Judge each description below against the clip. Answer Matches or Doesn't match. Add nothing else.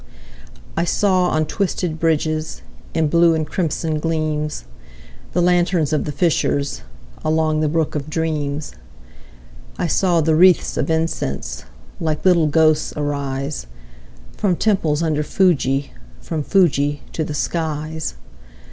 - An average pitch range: Doesn't match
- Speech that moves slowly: Matches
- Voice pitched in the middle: Matches